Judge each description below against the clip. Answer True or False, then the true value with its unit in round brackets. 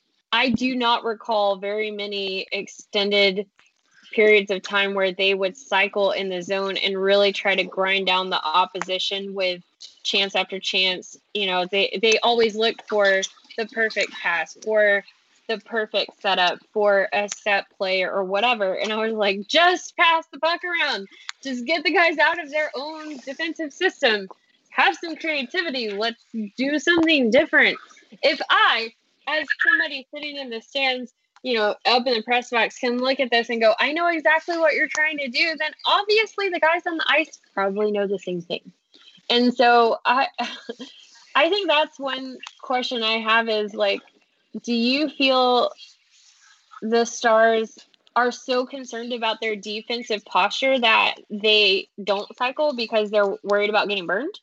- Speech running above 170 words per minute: False (165 wpm)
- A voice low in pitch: False (230 Hz)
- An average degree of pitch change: False (6.3 semitones)